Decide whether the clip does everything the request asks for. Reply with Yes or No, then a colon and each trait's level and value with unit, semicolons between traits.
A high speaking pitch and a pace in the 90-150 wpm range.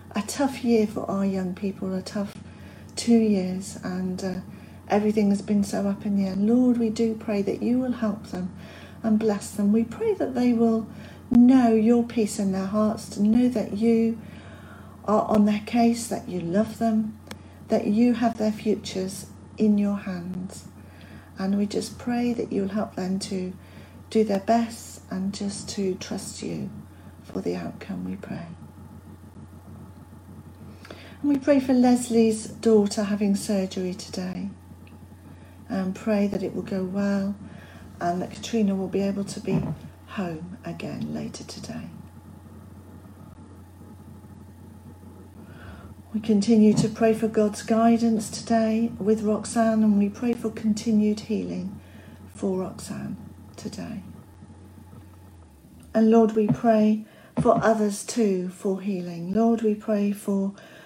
Yes: high, 200 Hz; average, 145 wpm